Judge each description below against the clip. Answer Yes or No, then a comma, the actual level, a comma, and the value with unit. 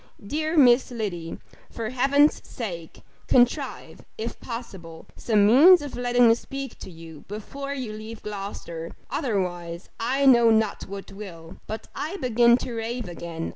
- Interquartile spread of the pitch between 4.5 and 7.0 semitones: Yes, average, 4.9 semitones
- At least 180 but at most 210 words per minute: No, average, 145 wpm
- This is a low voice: No, high, 225 Hz